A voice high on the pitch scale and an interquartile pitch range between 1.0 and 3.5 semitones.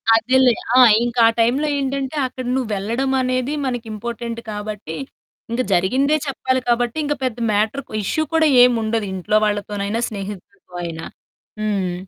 No: high, 230 Hz; average, 3.9 semitones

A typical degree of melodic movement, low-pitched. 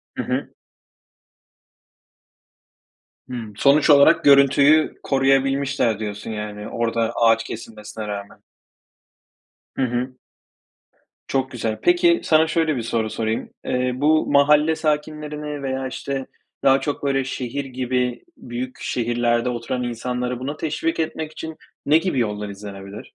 Yes: average, 3.9 semitones; low, 130 Hz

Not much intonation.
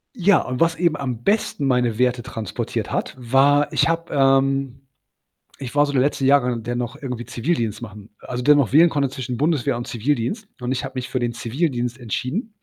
No: average, 3.2 semitones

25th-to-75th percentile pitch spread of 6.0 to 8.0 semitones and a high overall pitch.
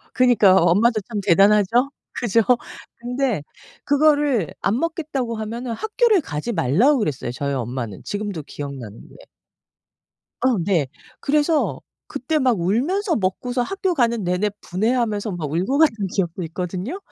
Yes: wide, 6.7 semitones; high, 220 Hz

